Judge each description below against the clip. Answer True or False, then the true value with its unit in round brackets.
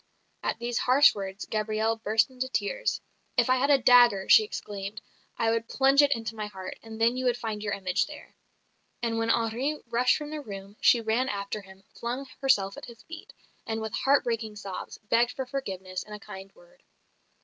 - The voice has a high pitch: True (225 Hz)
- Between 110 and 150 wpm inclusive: False (200 wpm)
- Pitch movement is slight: False (3.6 semitones)